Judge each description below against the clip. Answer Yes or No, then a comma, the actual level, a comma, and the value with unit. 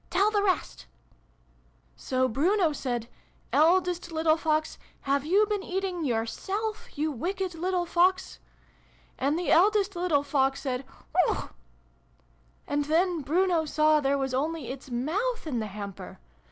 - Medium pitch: No, very high, 315 Hz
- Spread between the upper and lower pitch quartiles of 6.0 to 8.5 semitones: No, wide, 5.4 semitones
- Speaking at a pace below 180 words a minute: Yes, average, 155 wpm